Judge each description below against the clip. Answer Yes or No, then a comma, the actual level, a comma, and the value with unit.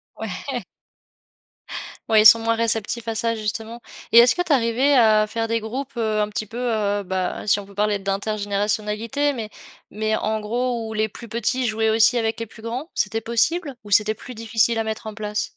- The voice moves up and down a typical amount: No, narrow, 1.7 semitones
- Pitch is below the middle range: No, high, 220 Hz